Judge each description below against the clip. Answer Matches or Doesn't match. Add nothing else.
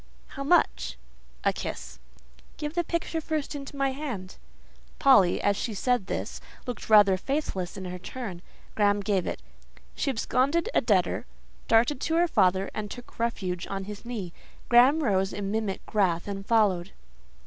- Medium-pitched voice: Doesn't match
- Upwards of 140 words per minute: Matches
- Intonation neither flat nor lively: Doesn't match